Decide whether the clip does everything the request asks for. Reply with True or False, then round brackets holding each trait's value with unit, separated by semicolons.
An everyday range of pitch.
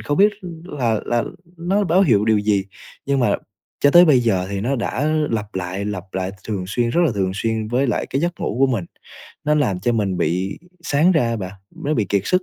False (6.4 semitones)